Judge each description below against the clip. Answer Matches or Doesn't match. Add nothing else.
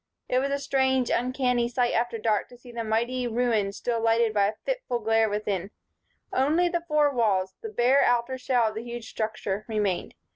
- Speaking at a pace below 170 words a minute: Doesn't match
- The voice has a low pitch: Doesn't match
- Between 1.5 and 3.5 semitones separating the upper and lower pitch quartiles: Matches